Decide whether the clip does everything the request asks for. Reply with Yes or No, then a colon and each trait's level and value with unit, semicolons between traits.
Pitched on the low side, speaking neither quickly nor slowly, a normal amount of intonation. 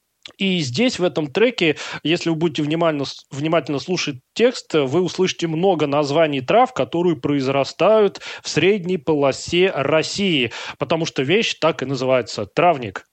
No: medium, 165 Hz; average, 135 wpm; average, 4.2 semitones